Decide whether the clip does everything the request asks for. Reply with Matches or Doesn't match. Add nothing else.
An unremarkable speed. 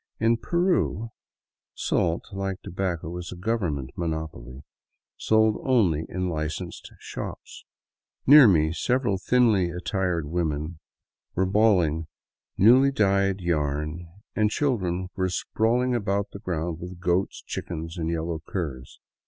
Doesn't match